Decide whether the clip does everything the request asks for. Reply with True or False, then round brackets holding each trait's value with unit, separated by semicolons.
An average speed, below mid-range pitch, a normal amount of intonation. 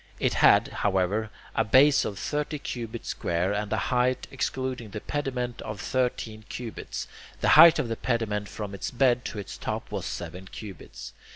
True (170 wpm; 115 Hz; 3.9 semitones)